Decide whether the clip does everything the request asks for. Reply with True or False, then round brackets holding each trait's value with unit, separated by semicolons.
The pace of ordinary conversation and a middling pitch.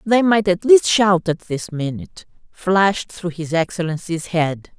True (165 wpm; 180 Hz)